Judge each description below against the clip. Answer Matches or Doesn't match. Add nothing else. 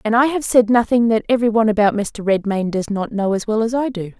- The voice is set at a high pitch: Matches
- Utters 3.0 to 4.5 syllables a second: Doesn't match